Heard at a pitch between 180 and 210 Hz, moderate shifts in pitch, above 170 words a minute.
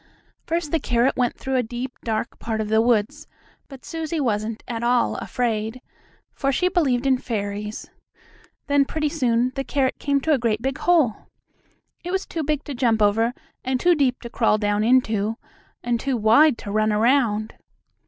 No: high, 245 Hz; average, 4.1 semitones; average, 180 wpm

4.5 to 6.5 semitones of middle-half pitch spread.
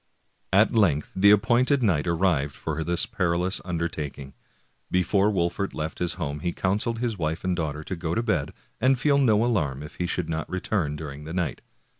Yes: average, 4.8 semitones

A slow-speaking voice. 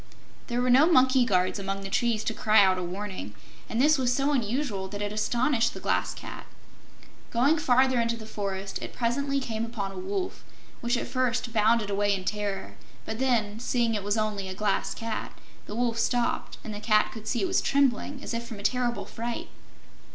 No: fast, 205 wpm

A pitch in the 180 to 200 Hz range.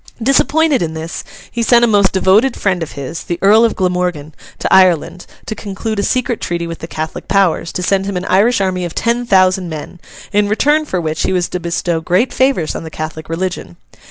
Yes: medium, 185 Hz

